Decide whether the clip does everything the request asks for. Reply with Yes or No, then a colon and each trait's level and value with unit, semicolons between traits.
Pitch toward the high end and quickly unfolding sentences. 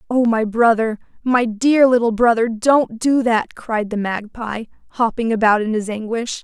No: high, 230 Hz; average, 170 wpm